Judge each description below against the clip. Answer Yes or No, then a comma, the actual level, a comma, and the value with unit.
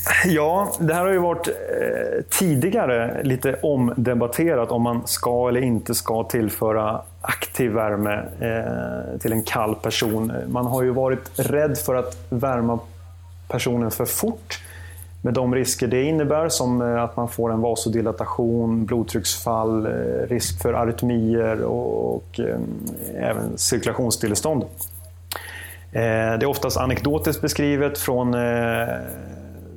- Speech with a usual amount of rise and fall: Yes, average, 3.3 semitones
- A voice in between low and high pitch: No, low, 115 Hz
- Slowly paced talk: Yes, slow, 115 wpm